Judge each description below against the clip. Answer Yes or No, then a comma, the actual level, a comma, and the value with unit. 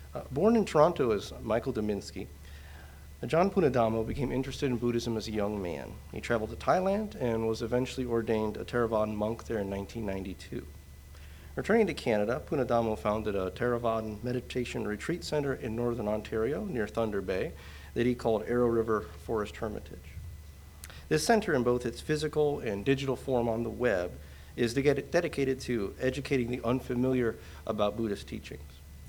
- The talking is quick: No, average, 155 wpm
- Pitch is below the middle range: Yes, low, 115 Hz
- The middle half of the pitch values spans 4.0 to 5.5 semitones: Yes, average, 4.5 semitones